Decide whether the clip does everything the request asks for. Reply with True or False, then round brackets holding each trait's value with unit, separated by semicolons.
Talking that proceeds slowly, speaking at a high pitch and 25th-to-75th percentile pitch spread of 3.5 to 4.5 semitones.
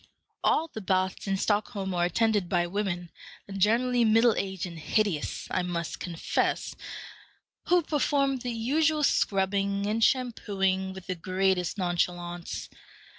True (125 wpm; 195 Hz; 4.0 semitones)